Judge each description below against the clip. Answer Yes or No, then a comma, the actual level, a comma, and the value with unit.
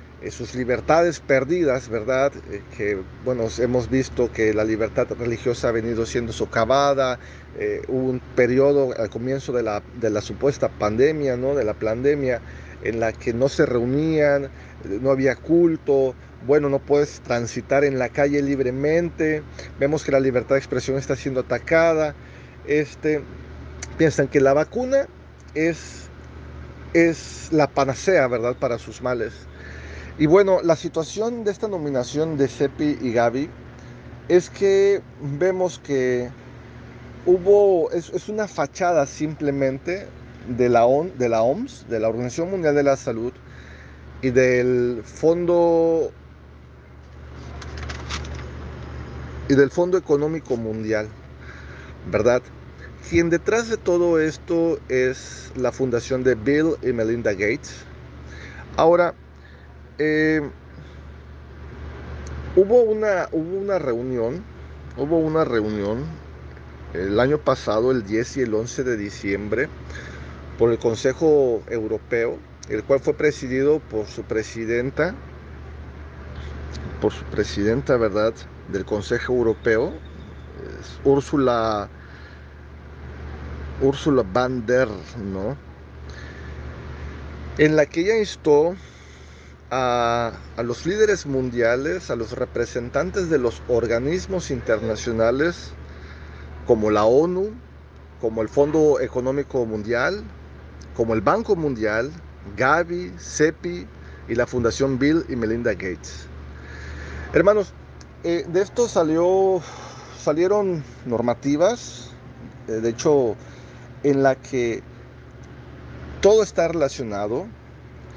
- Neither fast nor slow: No, slow, 115 wpm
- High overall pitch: No, low, 120 Hz